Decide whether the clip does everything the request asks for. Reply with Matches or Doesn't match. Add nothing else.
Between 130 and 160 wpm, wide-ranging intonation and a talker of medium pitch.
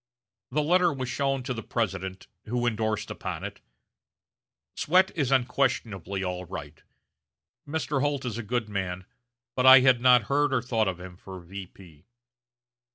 Doesn't match